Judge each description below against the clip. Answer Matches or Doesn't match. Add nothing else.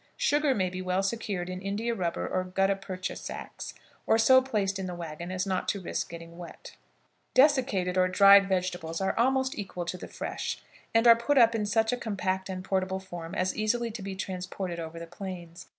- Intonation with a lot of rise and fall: Doesn't match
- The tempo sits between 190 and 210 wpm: Matches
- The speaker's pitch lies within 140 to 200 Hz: Matches